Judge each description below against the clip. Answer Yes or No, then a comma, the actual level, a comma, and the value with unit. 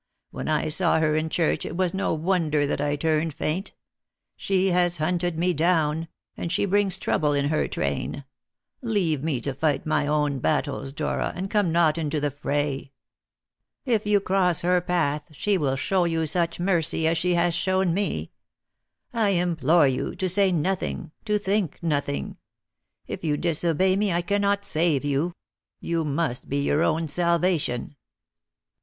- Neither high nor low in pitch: Yes, medium, 165 Hz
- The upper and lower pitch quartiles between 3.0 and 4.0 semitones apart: Yes, average, 3.5 semitones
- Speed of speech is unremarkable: Yes, average, 165 wpm